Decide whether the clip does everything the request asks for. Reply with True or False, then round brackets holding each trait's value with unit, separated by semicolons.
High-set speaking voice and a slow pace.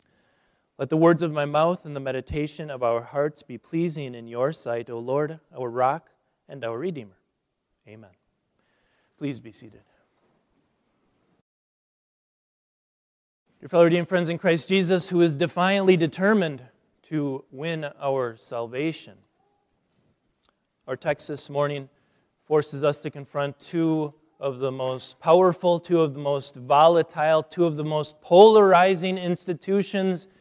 False (150 Hz; 130 wpm)